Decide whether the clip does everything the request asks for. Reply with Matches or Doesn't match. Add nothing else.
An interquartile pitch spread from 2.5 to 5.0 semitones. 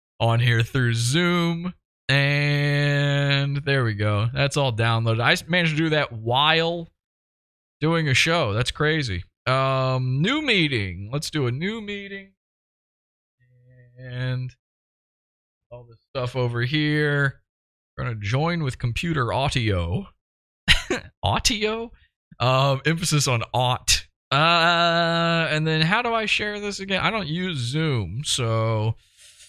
Doesn't match